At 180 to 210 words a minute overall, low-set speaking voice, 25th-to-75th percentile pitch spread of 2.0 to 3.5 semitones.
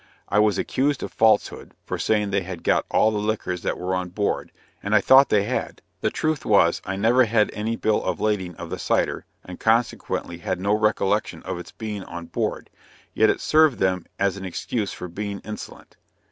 Yes: average, 200 wpm; low, 105 Hz; average, 2.8 semitones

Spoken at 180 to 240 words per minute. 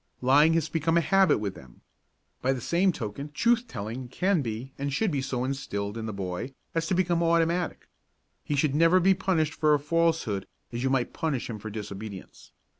Yes: average, 195 wpm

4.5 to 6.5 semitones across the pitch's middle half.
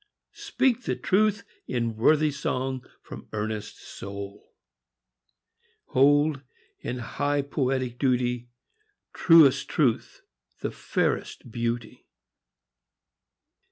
No: average, 3.7 semitones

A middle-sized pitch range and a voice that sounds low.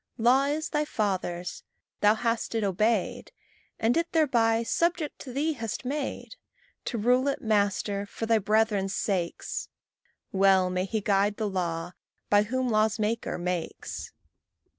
No: average, 4.0 semitones; high, 220 Hz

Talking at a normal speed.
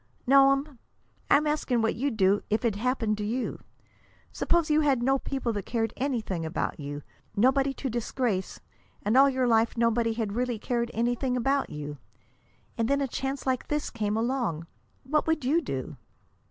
Yes: average, 170 wpm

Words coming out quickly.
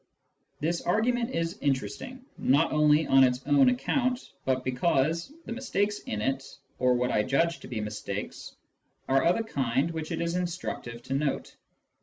No: average, 165 wpm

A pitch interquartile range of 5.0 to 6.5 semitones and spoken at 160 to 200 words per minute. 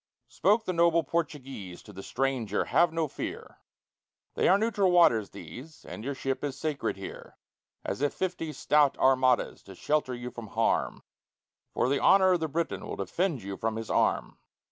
Yes: wide, 5.6 semitones; average, 175 wpm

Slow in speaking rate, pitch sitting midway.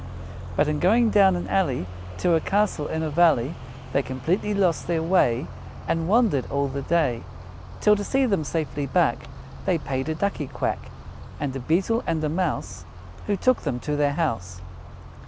No: average, 175 wpm; medium, 160 Hz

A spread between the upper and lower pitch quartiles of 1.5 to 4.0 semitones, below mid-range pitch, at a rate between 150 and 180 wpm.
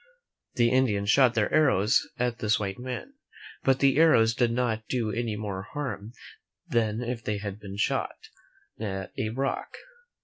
Yes: average, 3.1 semitones; low, 115 Hz; average, 160 wpm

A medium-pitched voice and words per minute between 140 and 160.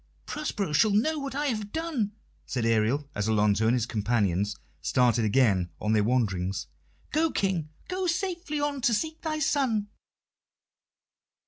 Yes: medium, 170 Hz; average, 145 wpm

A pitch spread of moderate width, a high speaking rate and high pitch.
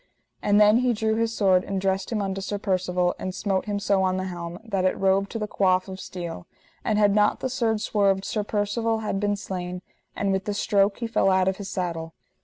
No: narrow, 2.0 semitones; fast, 230 wpm; high, 195 Hz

